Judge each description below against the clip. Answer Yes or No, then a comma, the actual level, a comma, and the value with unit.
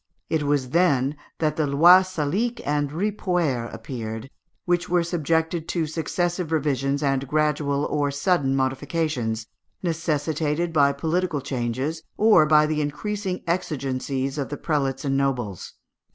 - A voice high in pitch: No, medium, 150 Hz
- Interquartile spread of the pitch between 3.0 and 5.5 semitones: Yes, average, 3.5 semitones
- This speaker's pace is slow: Yes, slow, 130 wpm